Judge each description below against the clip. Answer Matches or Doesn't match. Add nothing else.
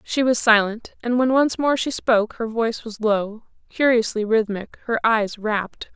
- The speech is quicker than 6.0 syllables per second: Doesn't match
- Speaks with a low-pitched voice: Doesn't match